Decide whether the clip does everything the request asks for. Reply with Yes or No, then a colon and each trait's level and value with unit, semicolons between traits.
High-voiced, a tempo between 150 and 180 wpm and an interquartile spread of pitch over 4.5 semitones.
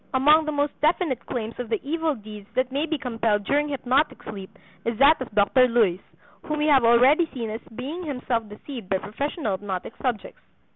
No: very high, 250 Hz; average, 190 wpm; average, 5.2 semitones